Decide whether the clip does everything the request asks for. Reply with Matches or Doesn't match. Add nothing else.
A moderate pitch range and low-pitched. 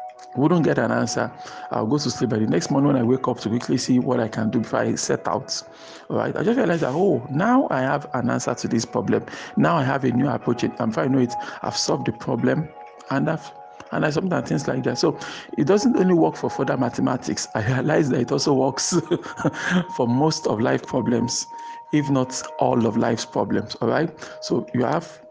Doesn't match